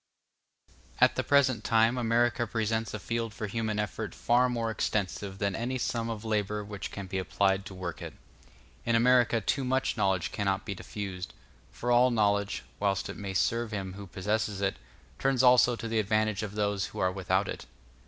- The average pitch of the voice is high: No, low, 105 Hz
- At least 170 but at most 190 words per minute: Yes, average, 185 wpm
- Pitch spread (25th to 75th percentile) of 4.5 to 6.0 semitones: No, average, 2.9 semitones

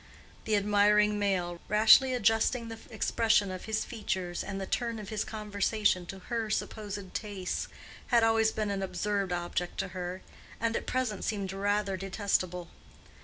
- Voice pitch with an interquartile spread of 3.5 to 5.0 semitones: No, narrow, 2.4 semitones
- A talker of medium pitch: No, high, 205 Hz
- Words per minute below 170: Yes, average, 155 wpm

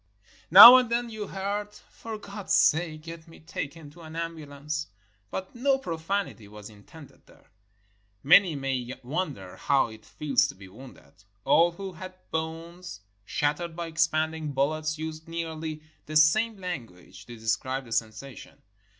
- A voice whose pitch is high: No, medium, 160 Hz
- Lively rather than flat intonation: No, average, 4.5 semitones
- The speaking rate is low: No, average, 150 wpm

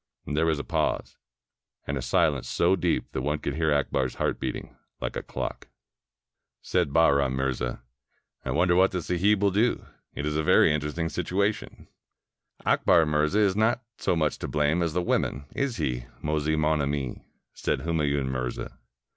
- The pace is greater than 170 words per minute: Yes, average, 180 wpm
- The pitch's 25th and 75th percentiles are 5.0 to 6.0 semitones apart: No, average, 3.9 semitones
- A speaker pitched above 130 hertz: No, very low, 75 Hz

